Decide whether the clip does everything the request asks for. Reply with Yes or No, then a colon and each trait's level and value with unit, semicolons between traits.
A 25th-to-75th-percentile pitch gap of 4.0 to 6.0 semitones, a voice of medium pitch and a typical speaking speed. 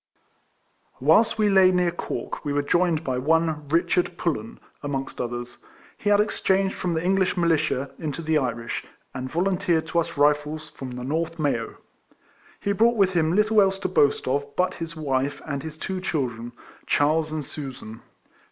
Yes: average, 4.4 semitones; medium, 160 Hz; average, 170 wpm